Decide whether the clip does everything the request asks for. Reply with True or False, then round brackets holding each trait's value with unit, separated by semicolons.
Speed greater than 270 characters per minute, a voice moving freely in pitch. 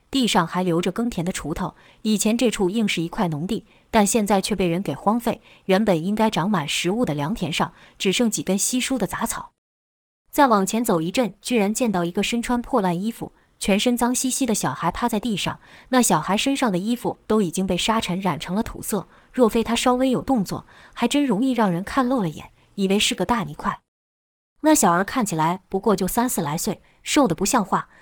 False (305 characters per minute; 4.9 semitones)